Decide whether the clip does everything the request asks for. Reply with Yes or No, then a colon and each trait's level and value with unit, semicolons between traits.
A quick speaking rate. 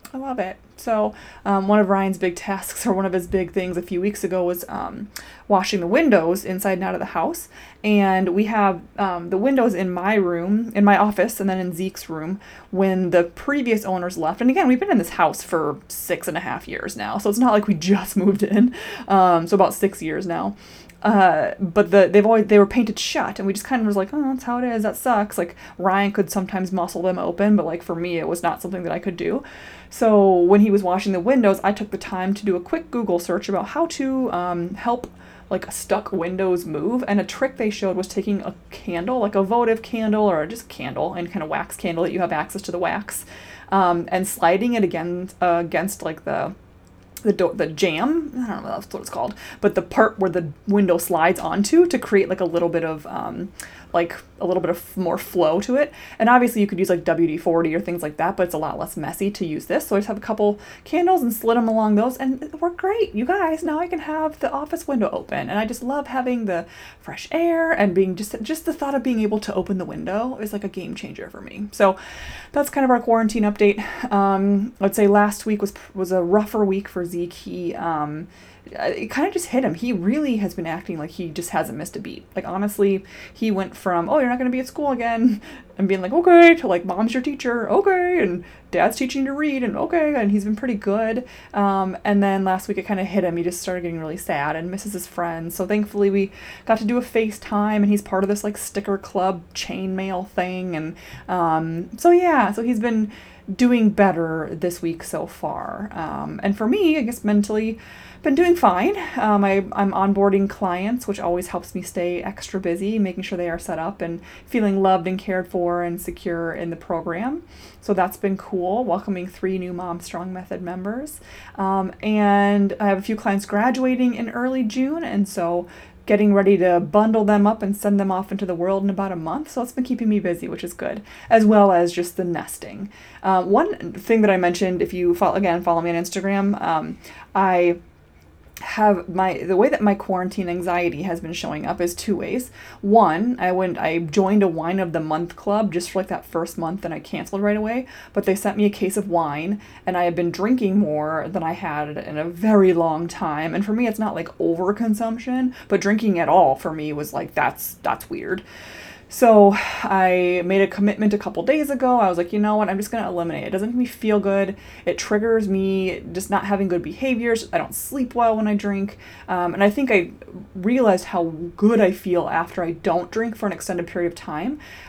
Yes: fast, 230 wpm